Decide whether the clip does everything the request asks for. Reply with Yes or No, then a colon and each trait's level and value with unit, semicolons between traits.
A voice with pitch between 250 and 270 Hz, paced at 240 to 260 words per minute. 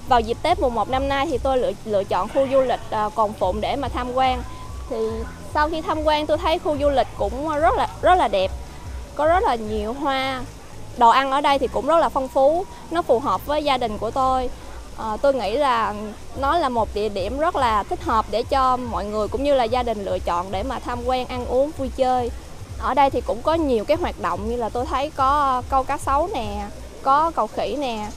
Yes: very high, 265 Hz; average, 245 wpm